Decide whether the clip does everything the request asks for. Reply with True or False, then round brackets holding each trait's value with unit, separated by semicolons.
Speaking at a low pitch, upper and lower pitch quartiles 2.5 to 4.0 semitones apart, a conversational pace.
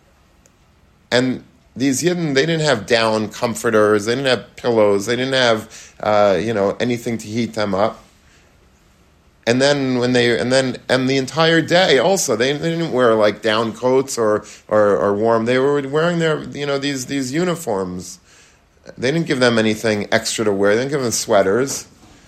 False (115 Hz; 4.4 semitones; 180 wpm)